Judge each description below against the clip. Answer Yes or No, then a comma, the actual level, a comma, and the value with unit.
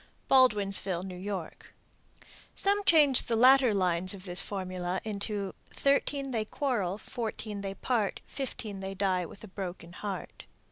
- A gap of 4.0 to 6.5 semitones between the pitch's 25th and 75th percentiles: Yes, average, 4.8 semitones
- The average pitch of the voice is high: Yes, high, 200 Hz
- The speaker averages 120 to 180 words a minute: Yes, slow, 135 wpm